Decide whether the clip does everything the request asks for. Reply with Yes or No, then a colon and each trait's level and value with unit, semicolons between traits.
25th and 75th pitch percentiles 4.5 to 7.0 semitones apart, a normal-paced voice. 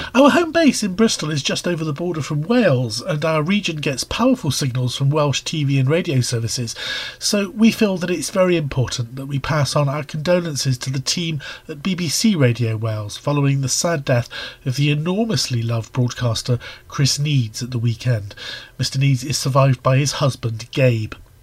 Yes: average, 5.0 semitones; average, 185 wpm